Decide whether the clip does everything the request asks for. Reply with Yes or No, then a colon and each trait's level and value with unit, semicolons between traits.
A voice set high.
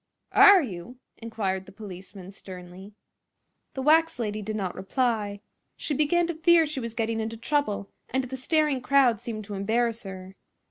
Yes: high, 225 Hz